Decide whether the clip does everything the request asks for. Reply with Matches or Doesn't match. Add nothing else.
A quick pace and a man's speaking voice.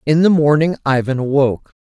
Doesn't match